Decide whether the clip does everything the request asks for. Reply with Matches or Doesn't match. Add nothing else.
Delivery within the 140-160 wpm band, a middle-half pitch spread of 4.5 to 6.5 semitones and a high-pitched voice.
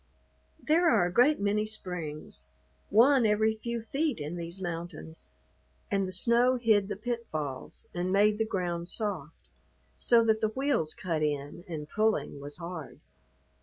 Matches